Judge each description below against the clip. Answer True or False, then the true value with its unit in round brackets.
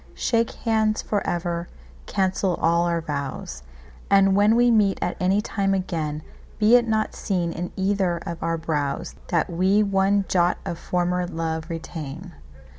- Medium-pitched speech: True (180 Hz)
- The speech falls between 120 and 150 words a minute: True (140 wpm)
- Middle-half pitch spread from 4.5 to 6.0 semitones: False (3.2 semitones)